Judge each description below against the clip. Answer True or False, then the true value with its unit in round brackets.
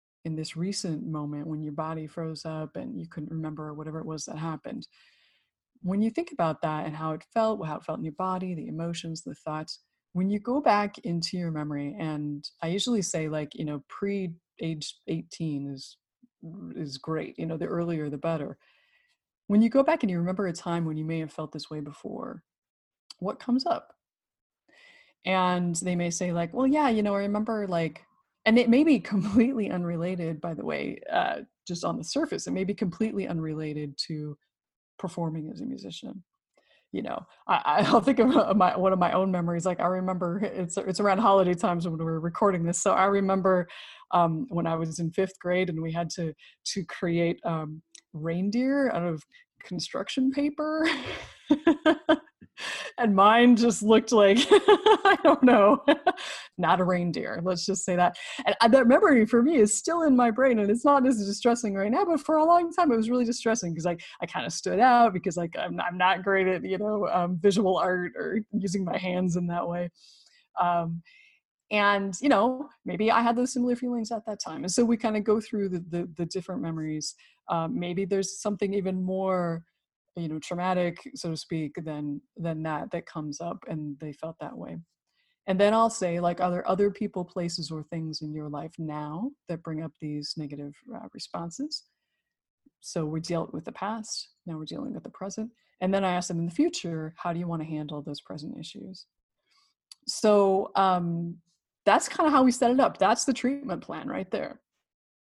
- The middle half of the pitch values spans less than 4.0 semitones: False (5.6 semitones)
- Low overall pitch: False (185 Hz)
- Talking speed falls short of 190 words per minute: False (200 wpm)